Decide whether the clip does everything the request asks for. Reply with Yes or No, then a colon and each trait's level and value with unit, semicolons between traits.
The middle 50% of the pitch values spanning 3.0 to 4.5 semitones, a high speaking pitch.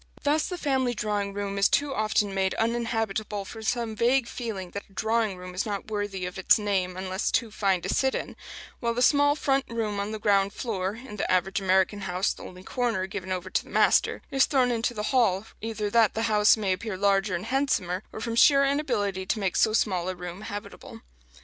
Yes: average, 3.4 semitones; high, 210 Hz